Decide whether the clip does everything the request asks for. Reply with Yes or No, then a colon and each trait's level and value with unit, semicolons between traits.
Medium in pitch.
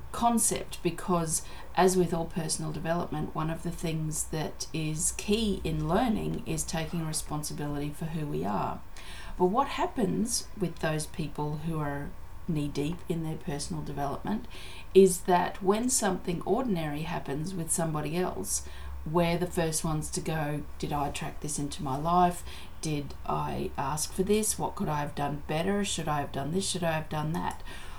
Yes: medium, 165 Hz